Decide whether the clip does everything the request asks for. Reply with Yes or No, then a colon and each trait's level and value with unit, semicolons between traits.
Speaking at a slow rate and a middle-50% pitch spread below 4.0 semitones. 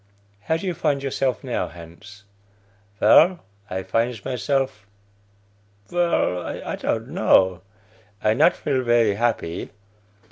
No: slow, 115 wpm; wide, 5.5 semitones